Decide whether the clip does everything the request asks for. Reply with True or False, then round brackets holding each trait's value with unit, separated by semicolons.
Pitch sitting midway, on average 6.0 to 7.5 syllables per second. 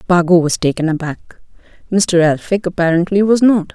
False (180 Hz; 5.0 syllables/s)